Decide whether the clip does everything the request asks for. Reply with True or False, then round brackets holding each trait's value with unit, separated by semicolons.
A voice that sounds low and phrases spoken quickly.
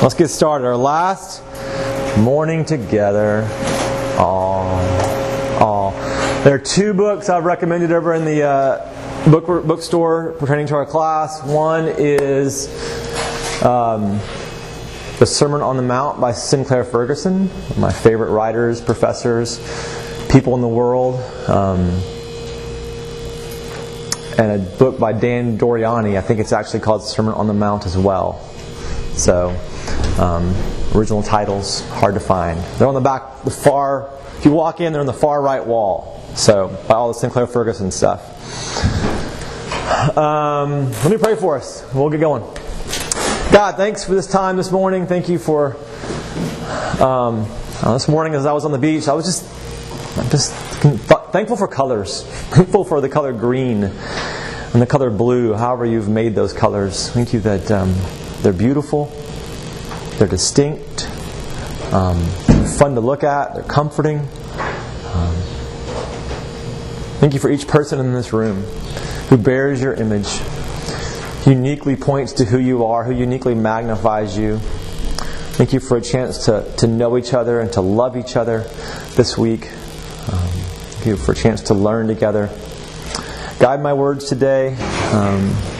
False (125 Hz; 150 wpm)